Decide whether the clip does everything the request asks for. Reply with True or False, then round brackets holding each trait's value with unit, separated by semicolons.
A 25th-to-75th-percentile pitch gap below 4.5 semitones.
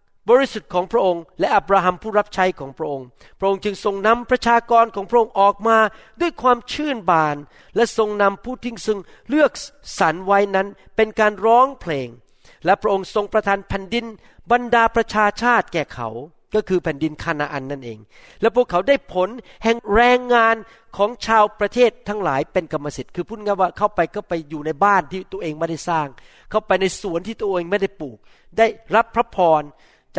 False (4.8 semitones)